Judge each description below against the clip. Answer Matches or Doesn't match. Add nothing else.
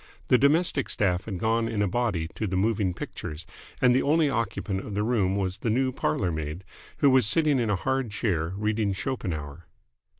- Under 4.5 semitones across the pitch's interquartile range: Doesn't match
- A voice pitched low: Matches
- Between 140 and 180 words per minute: Doesn't match